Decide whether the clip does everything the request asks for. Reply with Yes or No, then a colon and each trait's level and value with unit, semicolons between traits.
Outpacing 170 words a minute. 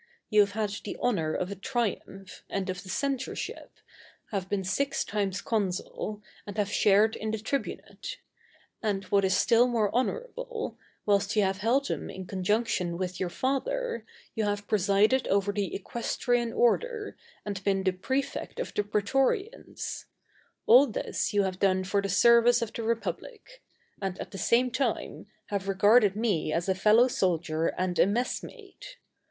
No: average, 160 wpm